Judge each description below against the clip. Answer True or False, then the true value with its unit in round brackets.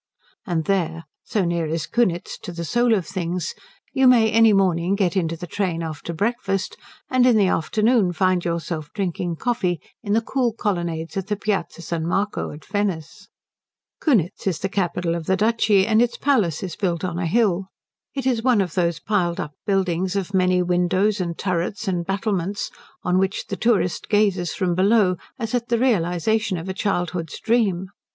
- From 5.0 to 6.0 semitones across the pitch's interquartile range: False (3.7 semitones)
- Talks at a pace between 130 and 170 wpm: False (180 wpm)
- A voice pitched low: False (190 Hz)